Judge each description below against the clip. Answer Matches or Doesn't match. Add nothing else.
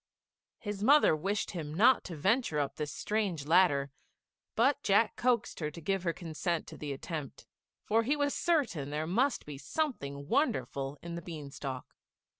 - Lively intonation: Matches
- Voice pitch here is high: Doesn't match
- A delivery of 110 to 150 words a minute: Doesn't match